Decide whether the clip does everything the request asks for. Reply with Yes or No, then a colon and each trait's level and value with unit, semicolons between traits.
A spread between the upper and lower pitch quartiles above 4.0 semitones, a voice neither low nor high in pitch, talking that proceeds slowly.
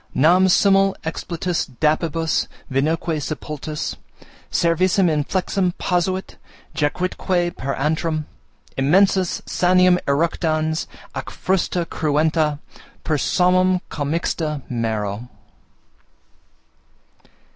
No: average, 3.2 semitones; medium, 165 Hz; slow, 75 wpm